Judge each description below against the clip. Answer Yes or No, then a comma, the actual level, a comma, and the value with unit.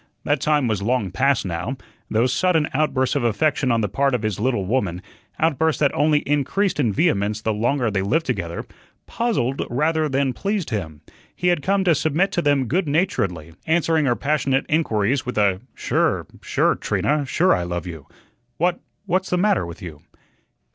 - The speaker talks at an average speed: Yes, average, 180 wpm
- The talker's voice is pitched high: No, low, 135 Hz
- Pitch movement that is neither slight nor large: No, wide, 7.0 semitones